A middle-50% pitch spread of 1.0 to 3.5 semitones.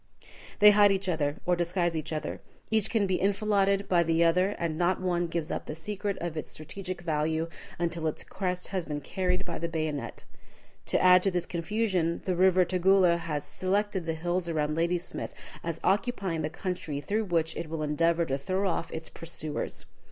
Yes: average, 2.7 semitones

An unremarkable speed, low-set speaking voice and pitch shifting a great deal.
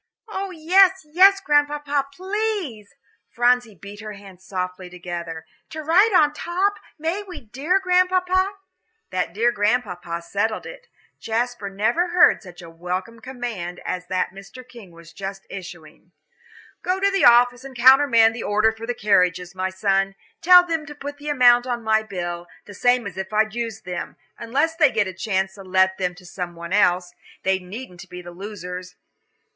No: average, 170 wpm; high, 220 Hz; wide, 8.0 semitones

